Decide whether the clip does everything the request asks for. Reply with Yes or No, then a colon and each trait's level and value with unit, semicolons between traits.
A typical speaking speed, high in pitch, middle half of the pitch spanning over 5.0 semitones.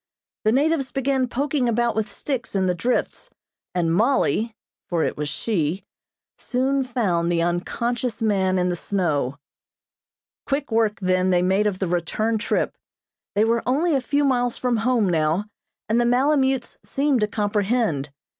Yes: average, 155 wpm; high, 220 Hz; wide, 5.6 semitones